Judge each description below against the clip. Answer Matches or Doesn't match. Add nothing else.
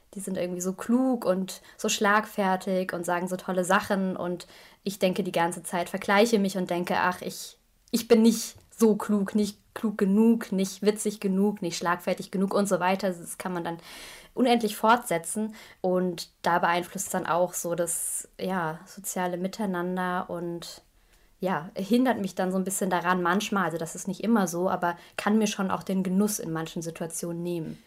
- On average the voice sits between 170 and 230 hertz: Matches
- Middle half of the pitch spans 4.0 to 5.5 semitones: Doesn't match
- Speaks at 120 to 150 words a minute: Doesn't match